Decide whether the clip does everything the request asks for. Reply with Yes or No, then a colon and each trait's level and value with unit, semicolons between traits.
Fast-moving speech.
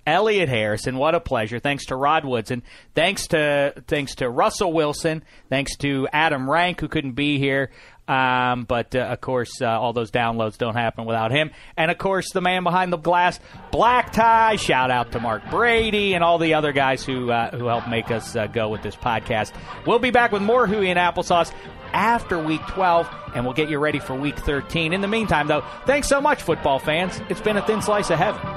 Yes: fast, 215 wpm